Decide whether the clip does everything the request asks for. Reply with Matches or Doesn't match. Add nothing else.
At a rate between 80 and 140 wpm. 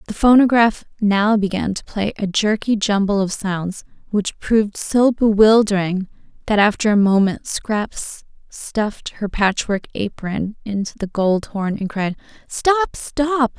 Matches